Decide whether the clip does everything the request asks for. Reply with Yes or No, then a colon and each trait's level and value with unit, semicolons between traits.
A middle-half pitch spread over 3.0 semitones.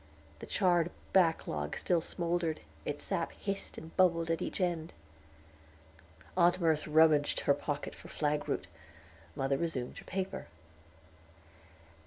No: average, 2.7 semitones